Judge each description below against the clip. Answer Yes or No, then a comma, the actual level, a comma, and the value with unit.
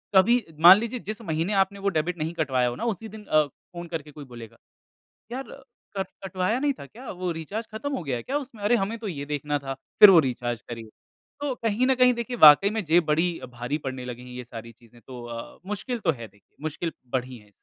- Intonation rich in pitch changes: Yes, wide, 9.0 semitones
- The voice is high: No, medium, 165 Hz